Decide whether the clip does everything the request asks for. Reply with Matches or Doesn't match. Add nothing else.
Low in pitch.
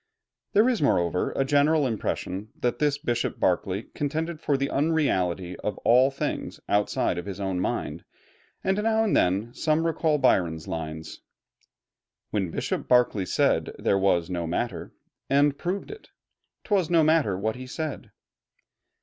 Matches